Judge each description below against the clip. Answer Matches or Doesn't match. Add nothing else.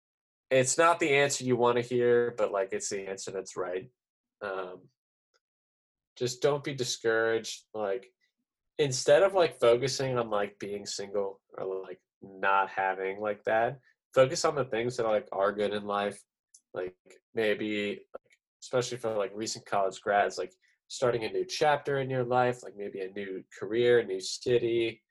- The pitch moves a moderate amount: Matches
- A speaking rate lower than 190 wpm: Matches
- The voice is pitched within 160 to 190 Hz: Doesn't match